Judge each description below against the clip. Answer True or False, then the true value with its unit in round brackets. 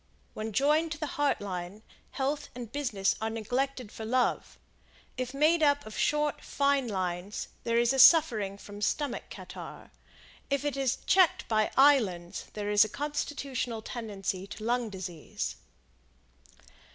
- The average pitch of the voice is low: False (240 Hz)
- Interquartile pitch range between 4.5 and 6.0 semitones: True (5.4 semitones)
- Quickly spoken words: False (140 wpm)